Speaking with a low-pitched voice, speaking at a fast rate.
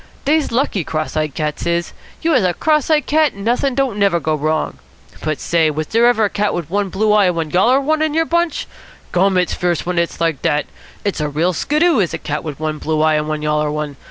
No: medium, 180 Hz; fast, 245 wpm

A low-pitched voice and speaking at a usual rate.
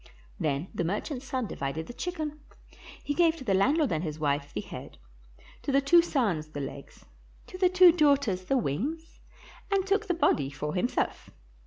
No: very high, 255 Hz; average, 180 wpm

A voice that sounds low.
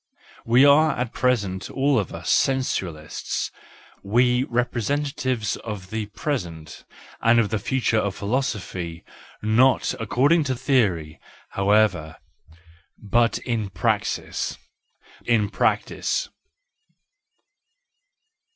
Yes: low, 115 Hz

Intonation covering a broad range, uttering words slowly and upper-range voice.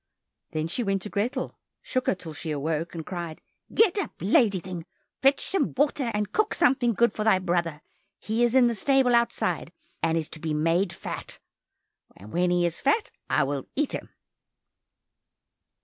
No: wide, 7.1 semitones; average, 175 wpm; high, 195 Hz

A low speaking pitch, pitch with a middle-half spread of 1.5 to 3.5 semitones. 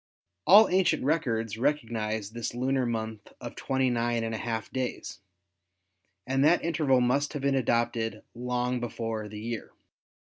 Yes: low, 120 Hz; average, 3.1 semitones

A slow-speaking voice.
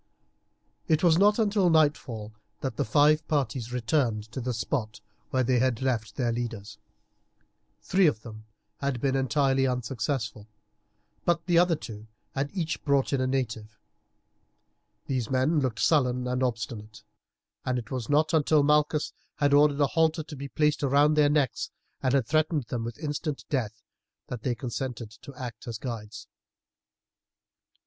No: average, 155 wpm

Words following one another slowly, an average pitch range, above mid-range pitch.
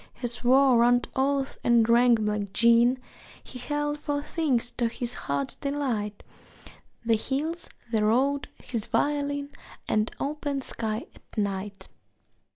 Yes: slow, 130 wpm; average, 4.2 semitones; high, 245 Hz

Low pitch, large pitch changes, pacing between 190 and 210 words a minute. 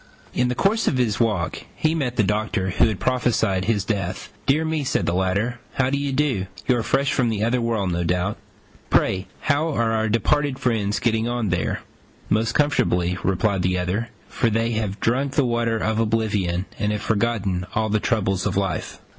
No: low, 110 Hz; average, 4.2 semitones; average, 195 wpm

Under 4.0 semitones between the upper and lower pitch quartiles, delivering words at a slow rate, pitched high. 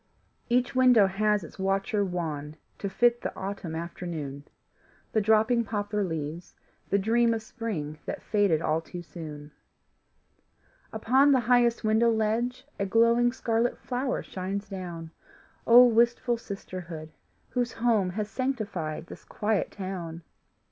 No: average, 5.2 semitones; slow, 130 wpm; high, 205 Hz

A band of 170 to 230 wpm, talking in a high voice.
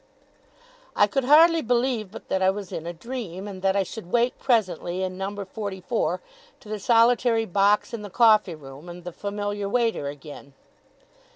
Yes: average, 180 wpm; high, 205 Hz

